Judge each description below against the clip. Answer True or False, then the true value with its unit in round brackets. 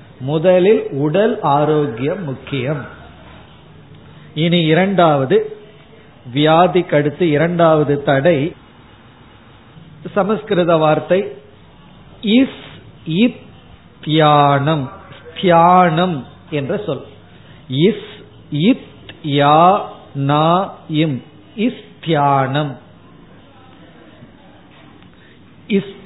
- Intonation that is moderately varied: True (4.5 semitones)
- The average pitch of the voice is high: False (155 Hz)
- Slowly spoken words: True (40 wpm)